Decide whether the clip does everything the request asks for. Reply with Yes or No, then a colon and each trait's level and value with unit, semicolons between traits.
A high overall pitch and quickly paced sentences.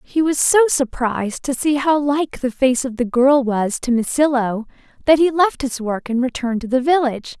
Yes: very high, 260 Hz; fast, 210 wpm